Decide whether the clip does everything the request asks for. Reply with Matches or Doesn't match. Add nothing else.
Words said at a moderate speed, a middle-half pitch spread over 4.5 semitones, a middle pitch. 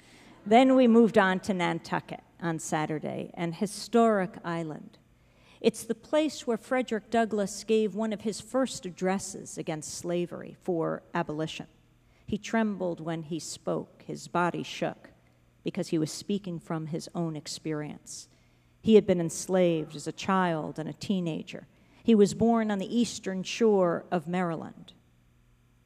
Matches